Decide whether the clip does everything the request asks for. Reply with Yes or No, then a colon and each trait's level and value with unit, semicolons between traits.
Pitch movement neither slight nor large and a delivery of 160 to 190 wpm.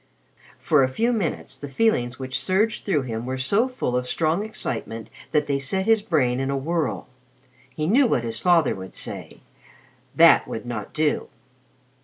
No: wide, 7.3 semitones; average, 175 wpm